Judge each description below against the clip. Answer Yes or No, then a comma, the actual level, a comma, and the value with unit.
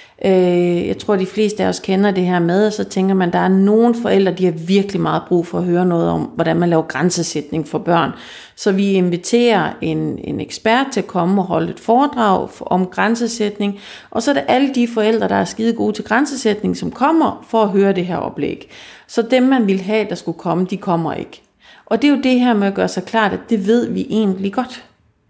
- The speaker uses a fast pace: Yes, fast, 235 wpm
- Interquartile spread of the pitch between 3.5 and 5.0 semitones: Yes, average, 4.2 semitones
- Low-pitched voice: No, high, 195 Hz